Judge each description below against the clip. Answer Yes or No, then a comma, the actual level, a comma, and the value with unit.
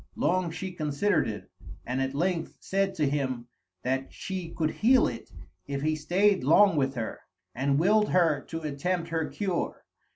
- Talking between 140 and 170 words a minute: Yes, average, 165 wpm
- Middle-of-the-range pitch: Yes, medium, 160 Hz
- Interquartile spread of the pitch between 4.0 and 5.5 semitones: Yes, average, 4.9 semitones